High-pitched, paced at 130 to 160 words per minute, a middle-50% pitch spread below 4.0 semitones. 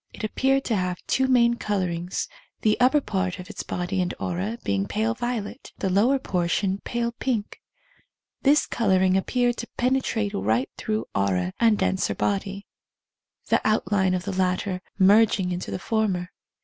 No: high, 200 Hz; average, 155 wpm; average, 4.3 semitones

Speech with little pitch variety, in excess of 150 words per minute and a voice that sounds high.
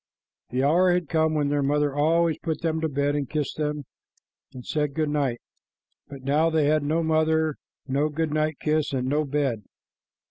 No: narrow, 1.8 semitones; average, 185 wpm; medium, 150 Hz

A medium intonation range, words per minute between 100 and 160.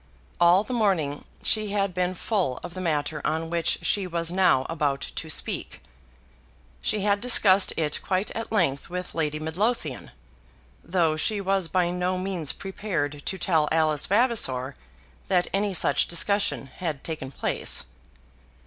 Yes: average, 4.1 semitones; average, 150 wpm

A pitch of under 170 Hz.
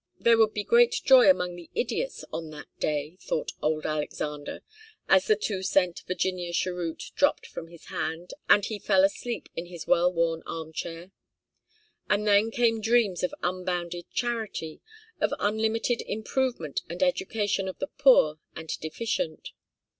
No: medium, 185 Hz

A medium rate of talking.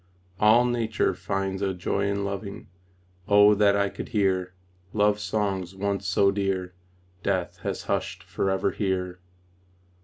No: slow, 130 wpm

